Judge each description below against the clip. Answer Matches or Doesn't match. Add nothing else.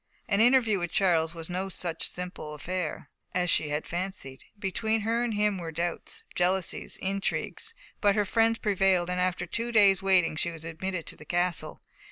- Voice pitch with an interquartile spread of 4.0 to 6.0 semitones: Doesn't match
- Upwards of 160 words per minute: Matches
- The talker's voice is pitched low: Doesn't match